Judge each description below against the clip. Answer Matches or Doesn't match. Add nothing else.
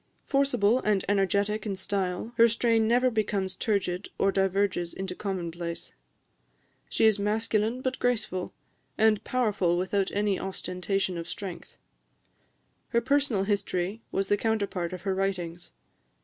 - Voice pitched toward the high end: Matches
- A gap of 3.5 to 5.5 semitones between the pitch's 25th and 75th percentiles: Doesn't match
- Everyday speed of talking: Doesn't match